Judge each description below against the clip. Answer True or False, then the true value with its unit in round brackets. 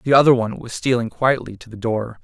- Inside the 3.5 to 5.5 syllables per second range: False (5.9 syllables/s)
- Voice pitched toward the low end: True (120 Hz)